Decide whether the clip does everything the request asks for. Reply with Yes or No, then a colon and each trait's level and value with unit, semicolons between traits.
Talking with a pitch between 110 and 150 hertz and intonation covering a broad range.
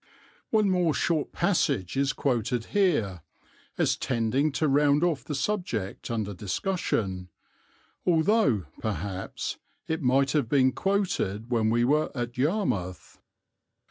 Yes: low, 135 Hz; wide, 6.7 semitones